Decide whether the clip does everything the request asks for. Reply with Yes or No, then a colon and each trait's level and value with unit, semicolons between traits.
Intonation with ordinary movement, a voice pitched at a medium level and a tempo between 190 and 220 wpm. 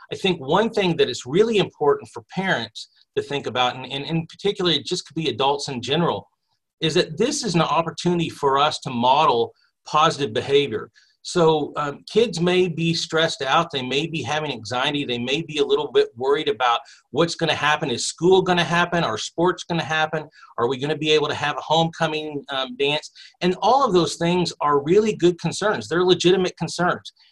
Yes: average, 3.6 semitones; medium, 165 Hz; average, 200 wpm